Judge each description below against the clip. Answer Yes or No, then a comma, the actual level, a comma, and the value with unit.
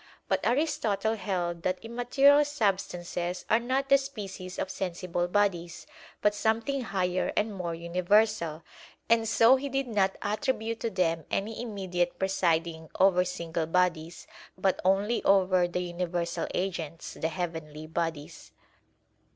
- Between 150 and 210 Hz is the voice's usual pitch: Yes, medium, 185 Hz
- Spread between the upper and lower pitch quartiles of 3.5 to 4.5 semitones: Yes, average, 4.2 semitones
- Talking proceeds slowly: Yes, slow, 130 wpm